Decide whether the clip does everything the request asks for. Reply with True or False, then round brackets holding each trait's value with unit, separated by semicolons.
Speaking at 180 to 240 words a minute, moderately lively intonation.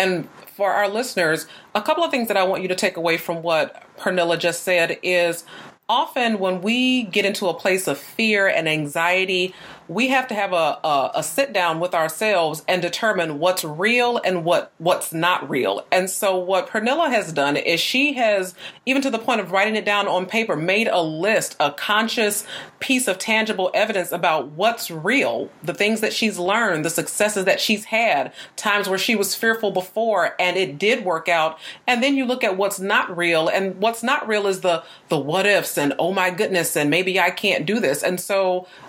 True (205 wpm; 3.9 semitones)